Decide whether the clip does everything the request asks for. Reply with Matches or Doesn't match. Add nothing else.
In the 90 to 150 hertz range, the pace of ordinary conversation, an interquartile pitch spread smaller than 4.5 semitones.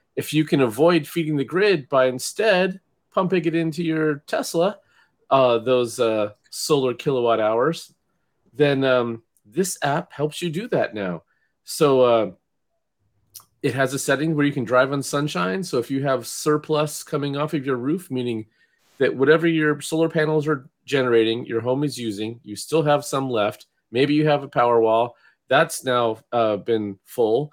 Doesn't match